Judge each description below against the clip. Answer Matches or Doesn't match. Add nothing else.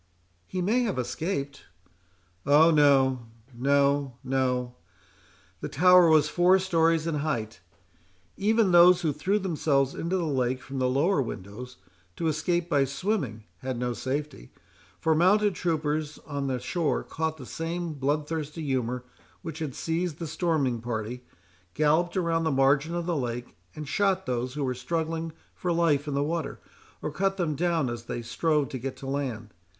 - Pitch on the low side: Doesn't match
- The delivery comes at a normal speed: Matches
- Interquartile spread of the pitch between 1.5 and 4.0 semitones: Doesn't match